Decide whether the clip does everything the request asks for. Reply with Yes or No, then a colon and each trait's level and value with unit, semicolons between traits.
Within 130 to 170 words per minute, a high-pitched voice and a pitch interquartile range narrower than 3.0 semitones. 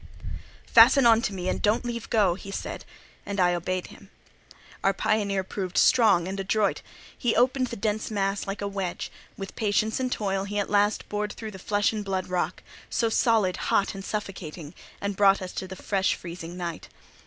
No: average, 180 wpm; high, 200 Hz; narrow, 2.4 semitones